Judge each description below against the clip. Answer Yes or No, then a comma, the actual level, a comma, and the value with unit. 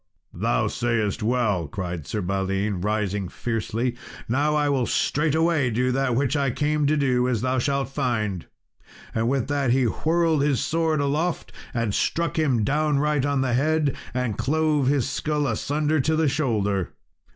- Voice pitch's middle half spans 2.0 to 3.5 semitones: No, average, 4.9 semitones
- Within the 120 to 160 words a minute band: Yes, average, 155 wpm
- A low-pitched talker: Yes, low, 130 Hz